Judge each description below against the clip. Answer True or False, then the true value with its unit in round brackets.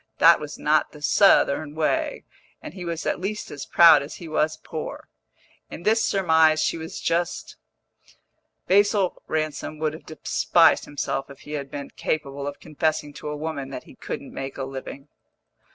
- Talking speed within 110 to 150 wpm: False (170 wpm)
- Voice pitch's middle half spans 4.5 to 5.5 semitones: False (2.5 semitones)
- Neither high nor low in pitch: True (155 Hz)